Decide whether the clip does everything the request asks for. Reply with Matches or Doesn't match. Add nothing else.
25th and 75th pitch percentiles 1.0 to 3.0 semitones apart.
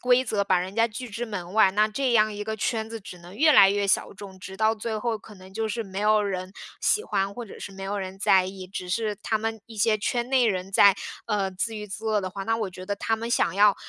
Matches